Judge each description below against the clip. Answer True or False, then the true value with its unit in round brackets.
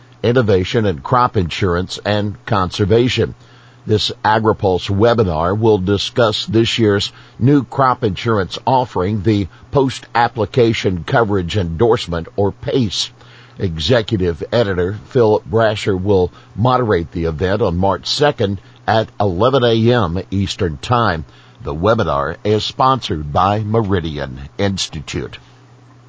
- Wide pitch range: False (4.1 semitones)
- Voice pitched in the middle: False (105 Hz)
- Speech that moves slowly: True (110 wpm)